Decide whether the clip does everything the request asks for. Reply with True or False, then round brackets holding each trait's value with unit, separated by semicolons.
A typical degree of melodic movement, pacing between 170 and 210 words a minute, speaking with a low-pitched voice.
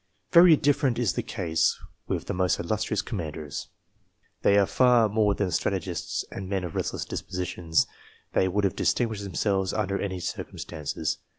False (3.3 semitones; 155 wpm; 100 Hz)